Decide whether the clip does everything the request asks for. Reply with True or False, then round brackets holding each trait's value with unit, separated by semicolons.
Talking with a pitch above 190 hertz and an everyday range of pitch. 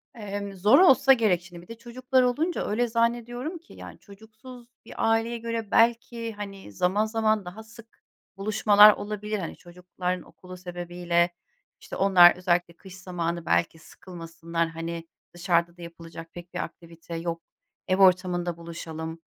False (185 Hz; 4.7 semitones)